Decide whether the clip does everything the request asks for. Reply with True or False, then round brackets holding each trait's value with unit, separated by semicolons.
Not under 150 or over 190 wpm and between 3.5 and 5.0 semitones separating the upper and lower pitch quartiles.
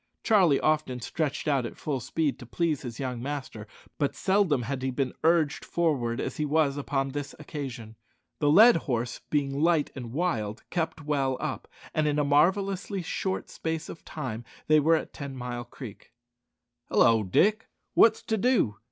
True (170 wpm; 4.2 semitones)